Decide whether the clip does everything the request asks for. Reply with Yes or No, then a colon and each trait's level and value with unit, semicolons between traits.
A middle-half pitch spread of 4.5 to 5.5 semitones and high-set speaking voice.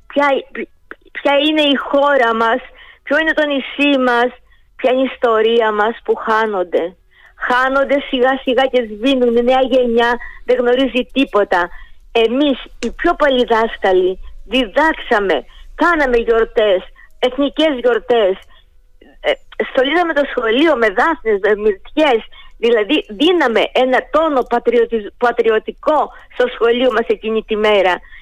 No: average, 3.8 semitones; very high, 250 Hz